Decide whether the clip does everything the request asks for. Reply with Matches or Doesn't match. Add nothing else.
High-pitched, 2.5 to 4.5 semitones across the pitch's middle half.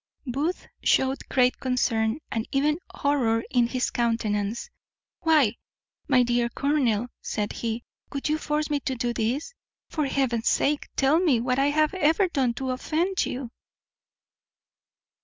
Matches